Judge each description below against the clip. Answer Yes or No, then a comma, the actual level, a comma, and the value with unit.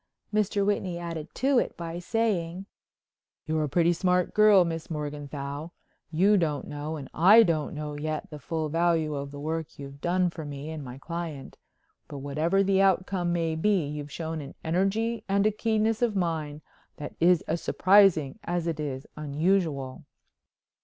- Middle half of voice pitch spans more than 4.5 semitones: No, average, 4.0 semitones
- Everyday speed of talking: Yes, average, 165 wpm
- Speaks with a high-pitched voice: No, medium, 165 Hz